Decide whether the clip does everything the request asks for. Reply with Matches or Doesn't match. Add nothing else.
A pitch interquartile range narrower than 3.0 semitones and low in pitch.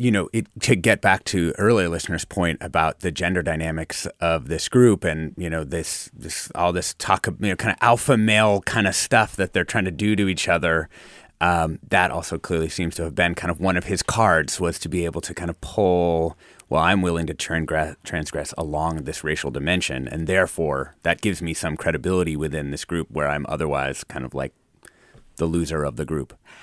Matches